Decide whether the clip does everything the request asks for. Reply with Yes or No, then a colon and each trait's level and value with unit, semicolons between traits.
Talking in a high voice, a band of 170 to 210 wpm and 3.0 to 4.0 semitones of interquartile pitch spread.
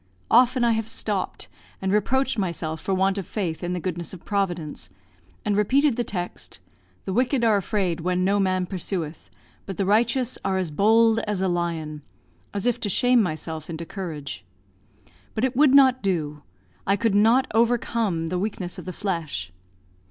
No: high, 195 Hz; average, 175 wpm; average, 4.6 semitones